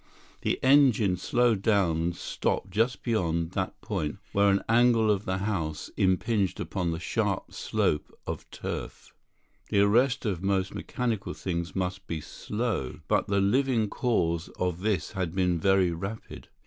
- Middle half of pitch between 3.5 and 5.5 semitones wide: Yes, average, 3.9 semitones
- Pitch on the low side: Yes, very low, 95 Hz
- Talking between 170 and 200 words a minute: No, average, 150 wpm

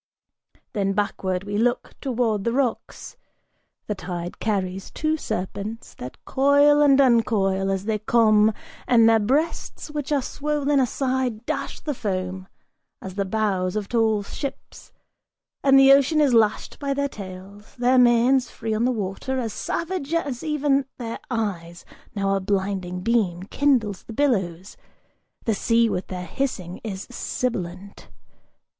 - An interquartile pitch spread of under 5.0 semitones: No, wide, 5.4 semitones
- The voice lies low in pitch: No, high, 225 Hz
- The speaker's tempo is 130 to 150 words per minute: Yes, average, 145 wpm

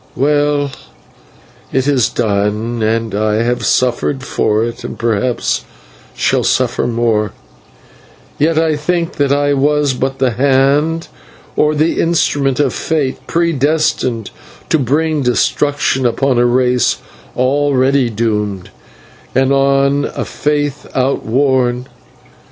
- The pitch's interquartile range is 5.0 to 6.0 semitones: No, average, 3.4 semitones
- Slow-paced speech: Yes, slow, 115 wpm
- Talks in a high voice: No, low, 135 Hz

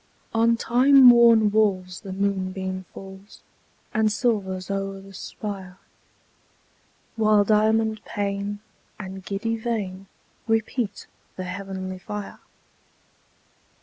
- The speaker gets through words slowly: Yes, slow, 95 wpm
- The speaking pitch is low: No, high, 200 Hz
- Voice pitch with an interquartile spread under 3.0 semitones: Yes, narrow, 2.5 semitones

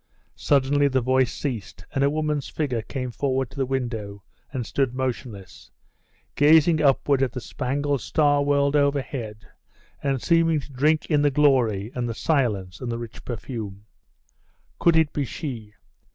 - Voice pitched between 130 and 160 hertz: Yes, low, 135 Hz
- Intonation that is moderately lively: Yes, average, 3.4 semitones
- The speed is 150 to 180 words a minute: Yes, average, 155 wpm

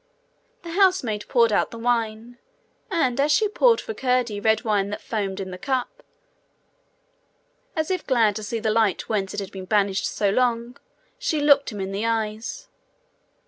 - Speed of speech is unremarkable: Yes, average, 175 wpm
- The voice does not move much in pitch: No, average, 4.4 semitones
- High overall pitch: Yes, high, 230 Hz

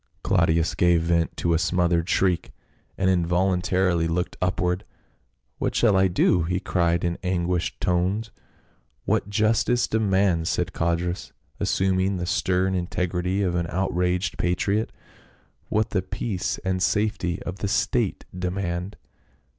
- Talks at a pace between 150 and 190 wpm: No, slow, 135 wpm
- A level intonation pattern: Yes, narrow, 1.6 semitones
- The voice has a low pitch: Yes, very low, 90 Hz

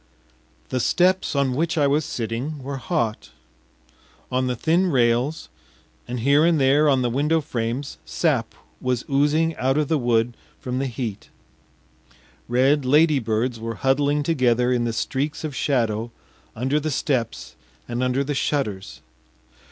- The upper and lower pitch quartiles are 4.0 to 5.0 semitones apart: No, average, 3.5 semitones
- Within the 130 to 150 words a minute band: Yes, average, 145 wpm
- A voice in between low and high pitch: No, low, 130 Hz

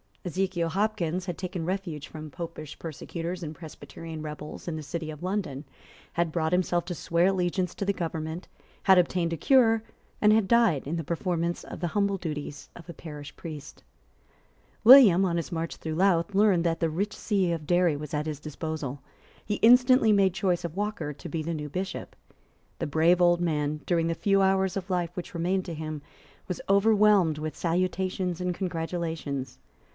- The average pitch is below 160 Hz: No, medium, 170 Hz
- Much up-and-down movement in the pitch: No, average, 3.2 semitones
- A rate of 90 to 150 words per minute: No, average, 180 wpm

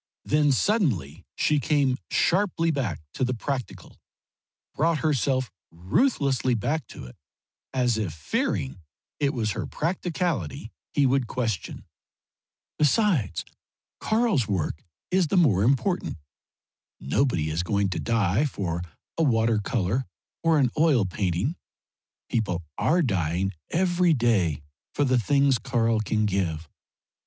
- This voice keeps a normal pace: No, slow, 125 wpm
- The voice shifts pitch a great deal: Yes, wide, 7.5 semitones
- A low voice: Yes, low, 125 Hz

